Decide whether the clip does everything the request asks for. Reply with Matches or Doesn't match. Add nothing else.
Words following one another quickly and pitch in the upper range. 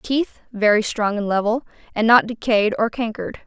Doesn't match